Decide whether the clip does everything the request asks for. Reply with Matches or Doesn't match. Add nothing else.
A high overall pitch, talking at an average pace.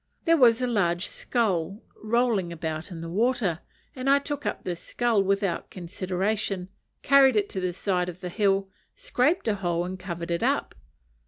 Matches